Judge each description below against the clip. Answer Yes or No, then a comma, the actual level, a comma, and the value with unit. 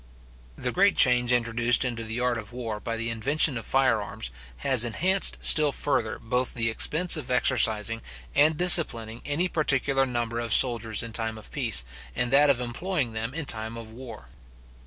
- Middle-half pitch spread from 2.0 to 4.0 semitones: Yes, average, 3.2 semitones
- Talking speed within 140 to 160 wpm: No, average, 180 wpm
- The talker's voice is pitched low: Yes, low, 120 Hz